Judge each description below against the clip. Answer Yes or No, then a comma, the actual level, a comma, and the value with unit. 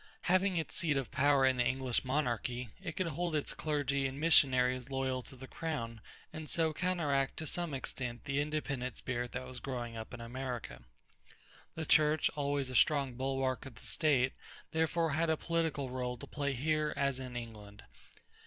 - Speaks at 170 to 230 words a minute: Yes, average, 180 wpm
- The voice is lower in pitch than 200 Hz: Yes, low, 135 Hz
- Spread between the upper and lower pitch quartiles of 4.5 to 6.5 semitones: No, average, 3.4 semitones